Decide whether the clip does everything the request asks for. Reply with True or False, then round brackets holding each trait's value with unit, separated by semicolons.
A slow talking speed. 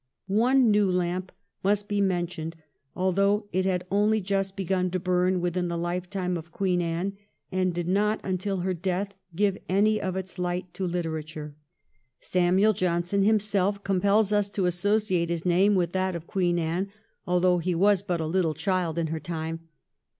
False (175 wpm)